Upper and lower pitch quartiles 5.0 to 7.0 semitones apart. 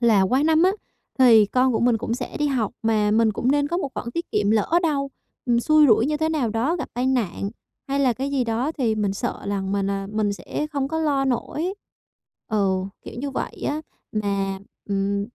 Yes: average, 5.3 semitones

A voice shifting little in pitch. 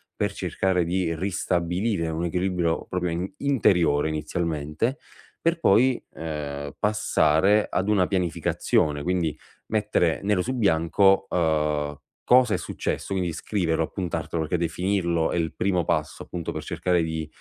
No: average, 3.3 semitones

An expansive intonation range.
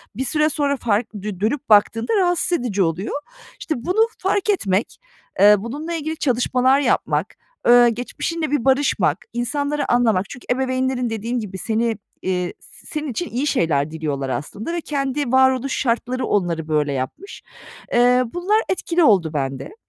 Yes: wide, 6.2 semitones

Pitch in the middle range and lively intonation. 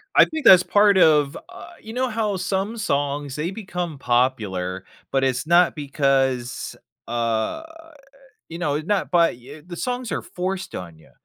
Yes: medium, 155 Hz; wide, 6.7 semitones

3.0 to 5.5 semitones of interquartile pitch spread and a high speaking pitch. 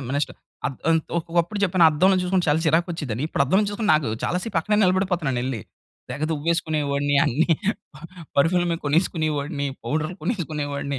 No: average, 3.8 semitones; medium, 160 Hz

